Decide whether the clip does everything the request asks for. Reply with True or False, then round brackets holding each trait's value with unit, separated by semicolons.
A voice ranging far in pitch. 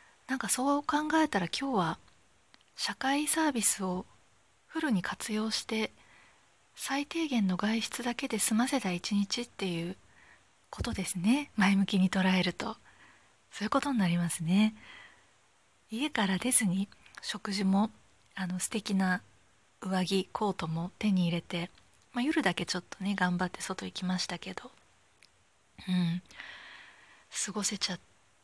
False (4.6 semitones)